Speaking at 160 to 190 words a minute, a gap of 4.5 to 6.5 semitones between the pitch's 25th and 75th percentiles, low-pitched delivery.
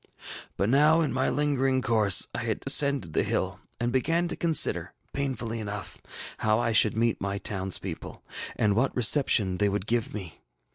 Yes: average, 170 wpm; average, 5.0 semitones; low, 115 Hz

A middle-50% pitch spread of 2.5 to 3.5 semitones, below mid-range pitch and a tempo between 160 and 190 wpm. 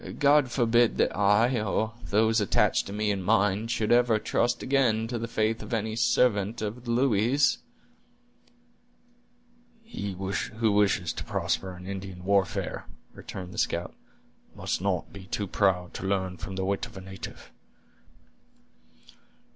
No: average, 3.2 semitones; low, 105 Hz; average, 145 wpm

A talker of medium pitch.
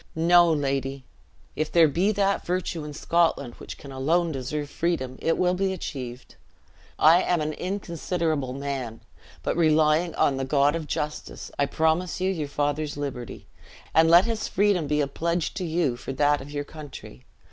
Yes: medium, 155 Hz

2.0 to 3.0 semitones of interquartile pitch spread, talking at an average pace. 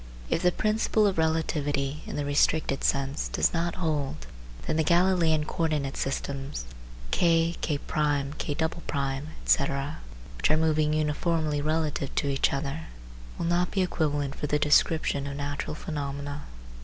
Yes: narrow, 2.4 semitones; average, 145 wpm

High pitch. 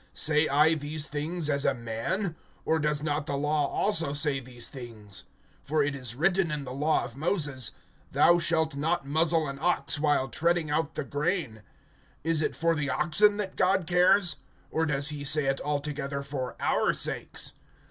No: medium, 150 Hz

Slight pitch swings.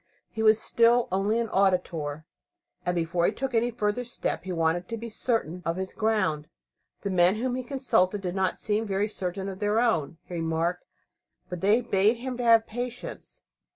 No: average, 4.4 semitones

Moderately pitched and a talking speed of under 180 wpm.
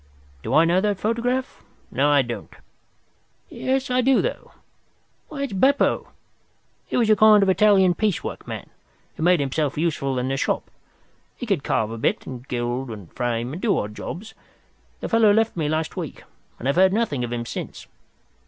No: medium, 175 Hz; average, 185 wpm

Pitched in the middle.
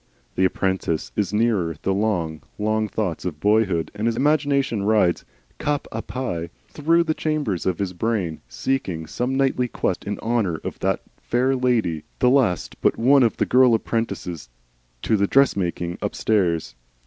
No: low, 110 Hz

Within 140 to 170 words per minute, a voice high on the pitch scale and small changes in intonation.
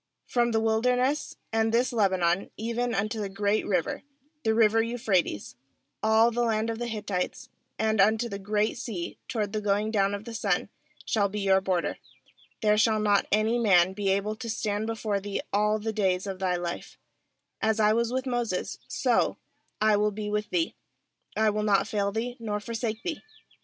No: average, 185 wpm; high, 215 Hz; narrow, 2.1 semitones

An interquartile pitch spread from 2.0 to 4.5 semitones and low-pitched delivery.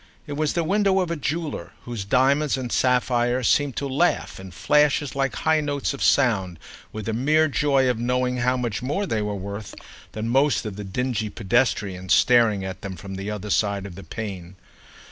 No: wide, 5.6 semitones; low, 125 Hz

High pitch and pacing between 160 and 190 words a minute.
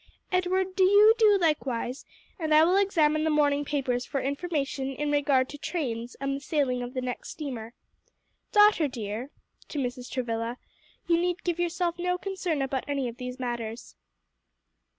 Yes: very high, 285 Hz; average, 165 wpm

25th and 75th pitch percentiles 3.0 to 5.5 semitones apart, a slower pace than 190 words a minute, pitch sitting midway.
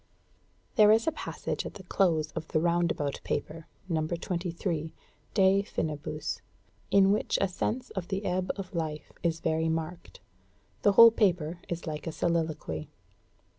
Yes: average, 3.3 semitones; average, 150 wpm; medium, 170 Hz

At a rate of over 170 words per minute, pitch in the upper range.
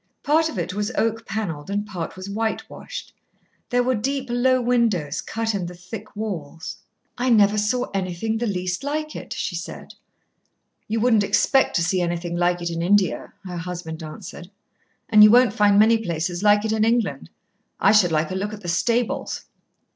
Yes: average, 185 wpm; high, 205 Hz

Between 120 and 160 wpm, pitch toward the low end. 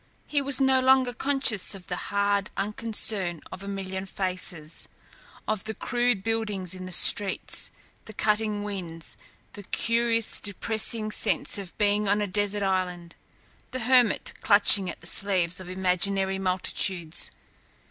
No: average, 140 wpm; high, 200 Hz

